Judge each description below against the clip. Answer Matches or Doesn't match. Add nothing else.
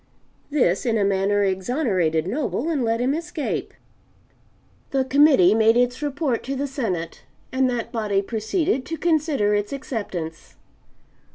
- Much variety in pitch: Matches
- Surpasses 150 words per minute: Doesn't match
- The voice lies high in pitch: Matches